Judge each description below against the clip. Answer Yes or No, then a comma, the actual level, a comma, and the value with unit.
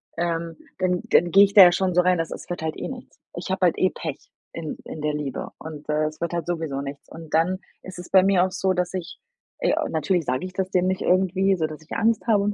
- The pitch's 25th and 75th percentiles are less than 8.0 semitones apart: Yes, average, 2.8 semitones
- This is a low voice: No, medium, 175 Hz